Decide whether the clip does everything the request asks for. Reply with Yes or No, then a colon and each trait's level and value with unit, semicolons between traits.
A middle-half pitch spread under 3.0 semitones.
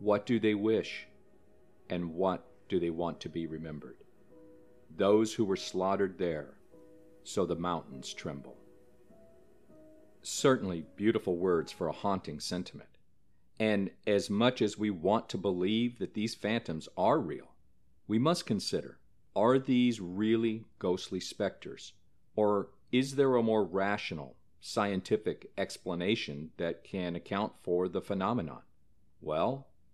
No: average, 4.4 semitones